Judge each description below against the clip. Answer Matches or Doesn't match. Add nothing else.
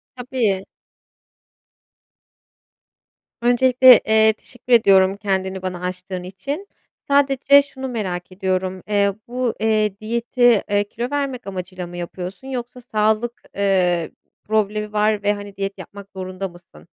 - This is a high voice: Matches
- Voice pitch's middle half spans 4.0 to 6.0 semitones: Matches